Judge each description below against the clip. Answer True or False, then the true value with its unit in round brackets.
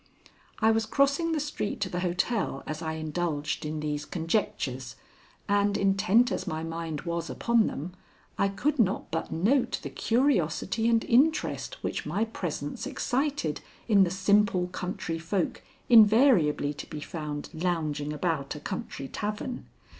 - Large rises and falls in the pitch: True (6.0 semitones)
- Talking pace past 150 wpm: False (145 wpm)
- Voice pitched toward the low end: False (185 Hz)